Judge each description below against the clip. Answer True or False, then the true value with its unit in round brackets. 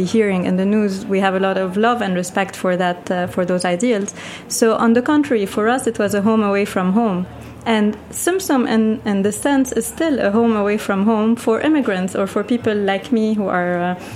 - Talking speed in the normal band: False (235 wpm)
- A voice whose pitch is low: False (210 Hz)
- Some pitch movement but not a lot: True (3.0 semitones)